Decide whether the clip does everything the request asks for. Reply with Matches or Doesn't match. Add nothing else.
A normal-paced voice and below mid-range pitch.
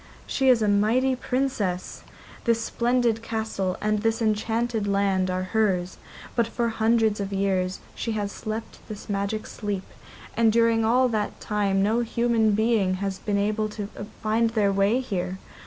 Doesn't match